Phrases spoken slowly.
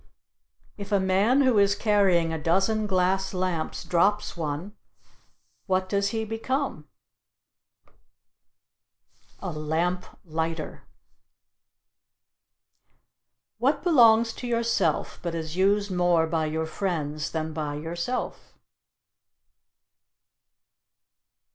Yes: slow, 90 wpm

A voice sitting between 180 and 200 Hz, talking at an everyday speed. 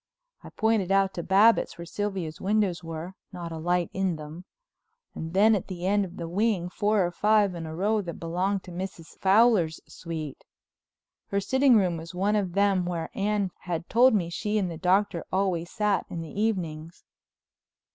Yes: medium, 185 Hz; average, 185 wpm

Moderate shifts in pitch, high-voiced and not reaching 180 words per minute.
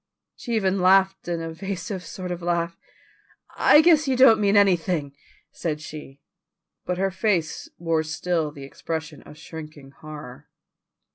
No: average, 3.7 semitones; medium, 170 Hz; average, 140 wpm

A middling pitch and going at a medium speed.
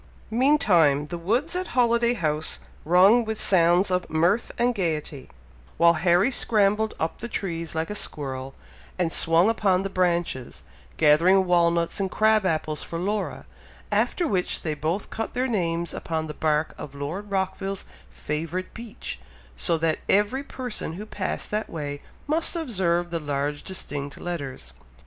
Yes: medium, 180 Hz; average, 150 wpm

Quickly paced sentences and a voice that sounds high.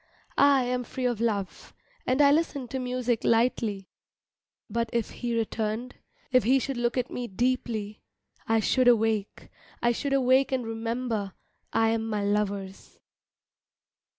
No: average, 145 wpm; high, 235 Hz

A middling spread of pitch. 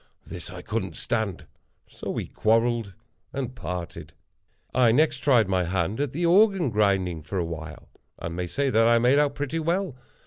No: wide, 7.5 semitones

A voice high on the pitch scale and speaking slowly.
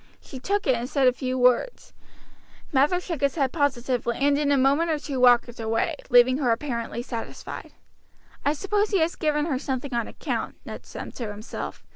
No: very high, 270 Hz; average, 190 wpm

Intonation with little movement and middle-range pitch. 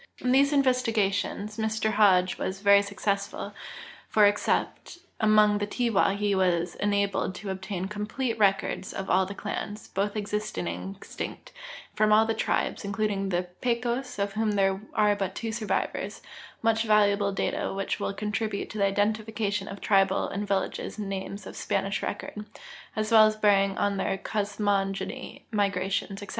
No: narrow, 1.6 semitones; high, 205 Hz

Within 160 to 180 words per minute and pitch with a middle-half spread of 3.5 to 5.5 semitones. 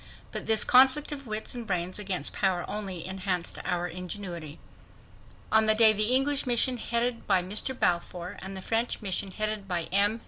Yes: average, 175 wpm; average, 4.1 semitones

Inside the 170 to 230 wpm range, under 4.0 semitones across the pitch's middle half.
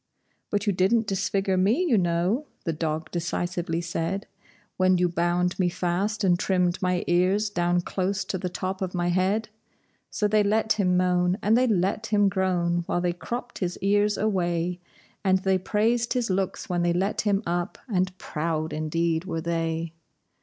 Yes: average, 175 wpm; narrow, 2.6 semitones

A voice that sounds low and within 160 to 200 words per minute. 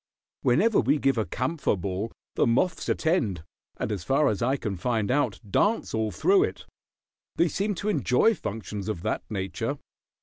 Yes: low, 120 Hz; average, 170 wpm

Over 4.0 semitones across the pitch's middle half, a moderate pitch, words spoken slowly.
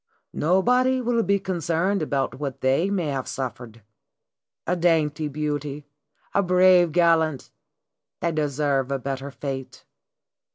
Yes: average, 4.7 semitones; medium, 155 Hz; slow, 120 wpm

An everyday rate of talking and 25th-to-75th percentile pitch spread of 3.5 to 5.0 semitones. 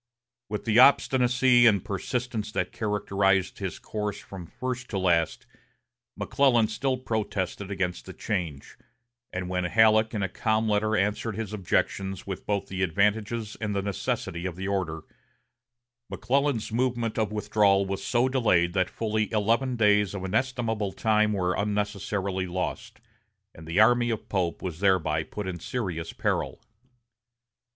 No: average, 145 wpm; average, 3.0 semitones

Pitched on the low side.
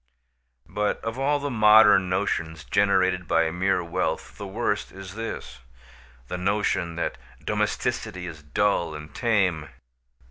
Yes: very low, 95 Hz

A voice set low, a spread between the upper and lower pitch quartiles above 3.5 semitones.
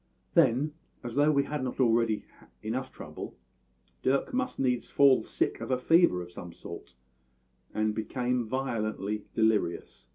Yes: low, 120 Hz; average, 4.1 semitones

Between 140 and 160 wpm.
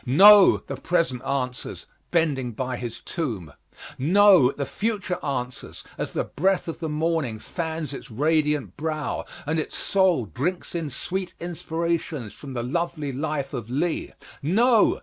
Yes: average, 145 wpm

